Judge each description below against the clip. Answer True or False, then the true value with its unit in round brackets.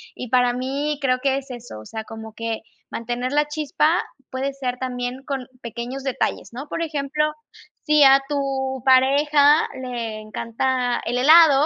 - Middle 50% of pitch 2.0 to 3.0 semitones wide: True (2.6 semitones)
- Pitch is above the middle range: True (265 Hz)